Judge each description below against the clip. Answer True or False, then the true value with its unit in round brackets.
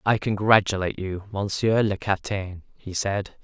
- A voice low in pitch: True (100 Hz)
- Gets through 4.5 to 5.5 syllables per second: True (5.1 syllables/s)